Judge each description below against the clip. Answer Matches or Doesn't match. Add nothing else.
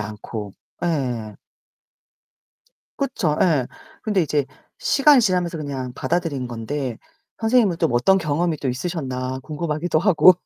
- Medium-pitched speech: Matches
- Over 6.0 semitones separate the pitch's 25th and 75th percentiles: Doesn't match